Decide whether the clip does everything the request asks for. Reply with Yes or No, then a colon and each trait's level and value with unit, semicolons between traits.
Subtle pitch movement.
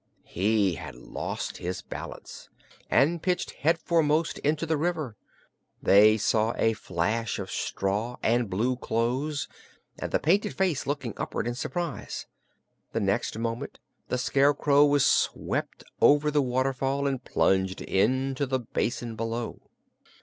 No: average, 4.7 semitones